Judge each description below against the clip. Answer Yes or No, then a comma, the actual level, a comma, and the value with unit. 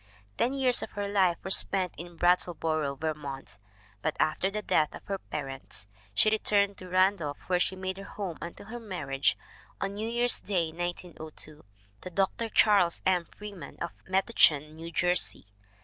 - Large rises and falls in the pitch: No, average, 4.1 semitones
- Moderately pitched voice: Yes, medium, 180 Hz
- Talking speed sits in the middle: Yes, average, 165 wpm